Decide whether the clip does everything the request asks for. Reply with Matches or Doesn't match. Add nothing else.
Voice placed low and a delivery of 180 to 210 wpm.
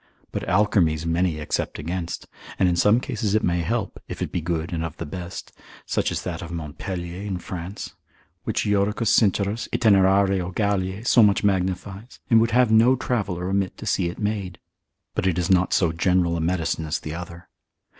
Matches